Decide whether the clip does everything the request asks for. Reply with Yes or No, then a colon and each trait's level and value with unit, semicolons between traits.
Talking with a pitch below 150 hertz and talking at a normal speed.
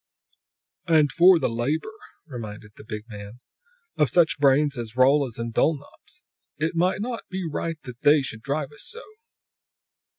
Yes: medium, 140 Hz; average, 145 wpm